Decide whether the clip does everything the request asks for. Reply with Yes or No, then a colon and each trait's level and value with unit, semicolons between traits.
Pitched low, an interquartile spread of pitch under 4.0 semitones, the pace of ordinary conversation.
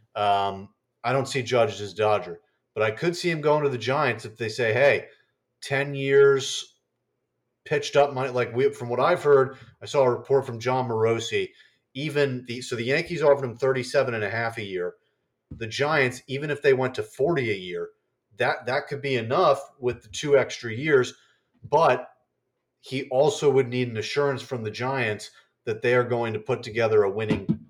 Yes: low, 130 Hz; average, 3.4 semitones; average, 195 wpm